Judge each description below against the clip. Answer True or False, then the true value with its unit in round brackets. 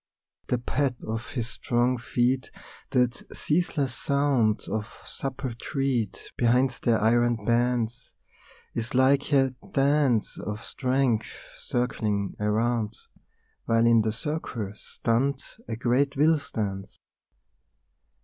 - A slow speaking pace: True (110 wpm)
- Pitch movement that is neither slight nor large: True (3.0 semitones)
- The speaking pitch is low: True (120 Hz)